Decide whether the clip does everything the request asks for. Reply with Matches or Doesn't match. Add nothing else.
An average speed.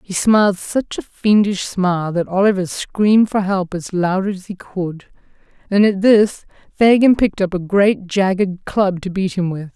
Matches